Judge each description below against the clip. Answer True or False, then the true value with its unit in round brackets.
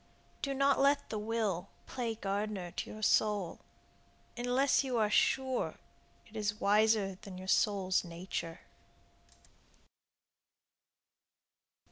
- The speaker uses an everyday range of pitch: True (4.0 semitones)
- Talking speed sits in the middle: False (105 wpm)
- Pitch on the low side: False (215 Hz)